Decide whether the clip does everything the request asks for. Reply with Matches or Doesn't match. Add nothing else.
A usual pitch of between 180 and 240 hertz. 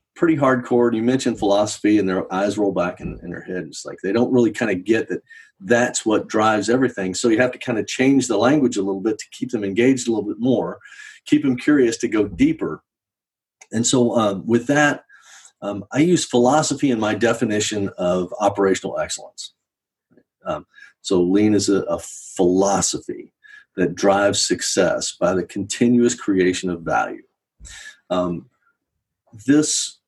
Doesn't match